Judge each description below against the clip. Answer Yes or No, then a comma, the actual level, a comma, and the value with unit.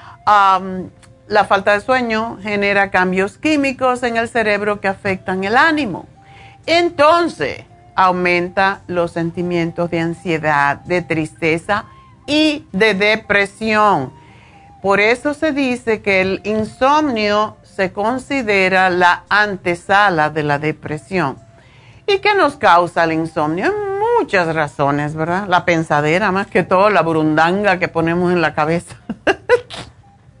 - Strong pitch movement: No, average, 4.9 semitones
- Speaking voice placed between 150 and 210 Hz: Yes, high, 190 Hz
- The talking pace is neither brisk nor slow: No, slow, 120 wpm